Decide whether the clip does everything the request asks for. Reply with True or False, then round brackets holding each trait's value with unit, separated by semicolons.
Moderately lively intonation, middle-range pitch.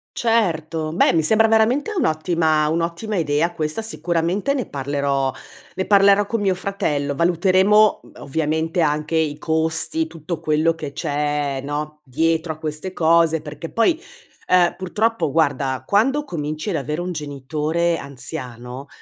True (3.8 semitones; 160 Hz)